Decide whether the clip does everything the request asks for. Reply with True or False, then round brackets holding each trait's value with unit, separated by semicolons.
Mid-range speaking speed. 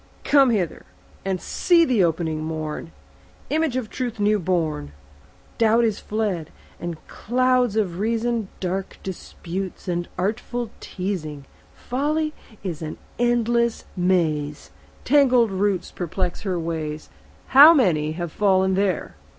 False (120 wpm)